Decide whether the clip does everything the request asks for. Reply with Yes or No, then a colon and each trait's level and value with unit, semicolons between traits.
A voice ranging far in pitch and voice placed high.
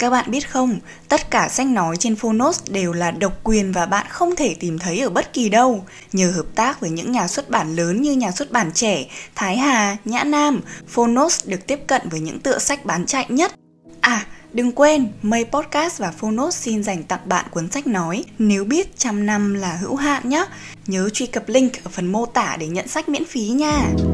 Yes: wide, 6.6 semitones; high, 230 Hz